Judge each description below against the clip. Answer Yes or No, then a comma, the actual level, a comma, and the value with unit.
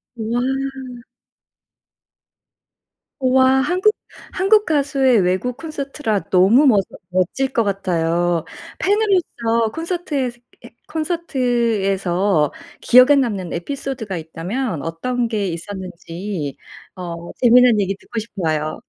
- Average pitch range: No, wide, 6.6 semitones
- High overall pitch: Yes, high, 230 Hz